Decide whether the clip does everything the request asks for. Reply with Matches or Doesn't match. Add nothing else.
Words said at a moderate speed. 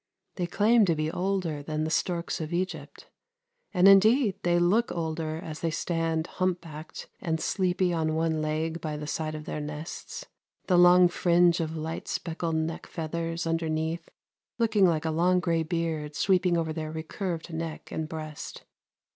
Matches